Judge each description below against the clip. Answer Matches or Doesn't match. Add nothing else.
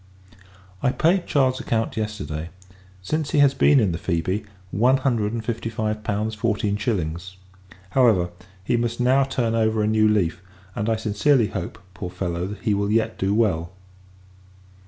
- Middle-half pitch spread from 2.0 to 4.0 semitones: Matches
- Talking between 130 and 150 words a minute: Doesn't match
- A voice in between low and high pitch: Doesn't match